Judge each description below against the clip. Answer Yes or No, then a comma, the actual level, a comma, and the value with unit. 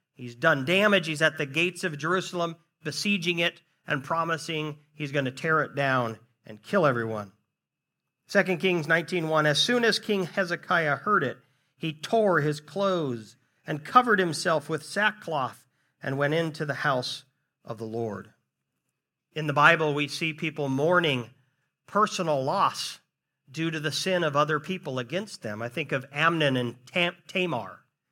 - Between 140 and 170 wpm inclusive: Yes, average, 160 wpm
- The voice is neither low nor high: Yes, medium, 155 Hz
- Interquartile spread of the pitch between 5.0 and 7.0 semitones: No, average, 3.9 semitones